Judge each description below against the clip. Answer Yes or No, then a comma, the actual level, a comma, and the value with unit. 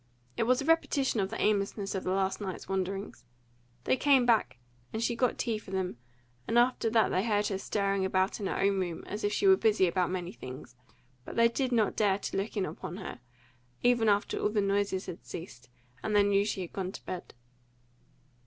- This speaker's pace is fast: Yes, fast, 215 wpm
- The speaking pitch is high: Yes, high, 200 Hz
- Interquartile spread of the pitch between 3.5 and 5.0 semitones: No, average, 3.0 semitones